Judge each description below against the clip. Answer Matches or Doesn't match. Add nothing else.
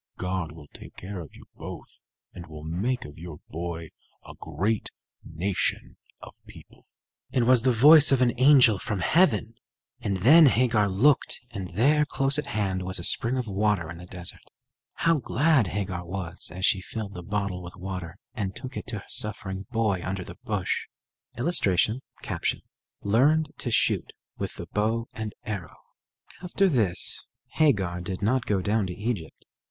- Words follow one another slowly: Doesn't match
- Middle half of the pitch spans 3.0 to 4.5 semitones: Doesn't match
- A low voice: Matches